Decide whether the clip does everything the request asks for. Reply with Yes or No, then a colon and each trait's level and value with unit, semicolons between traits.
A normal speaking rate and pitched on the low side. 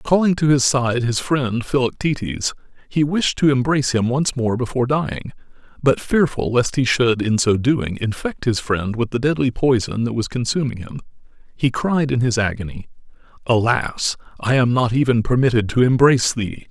Yes: average, 175 wpm; low, 125 Hz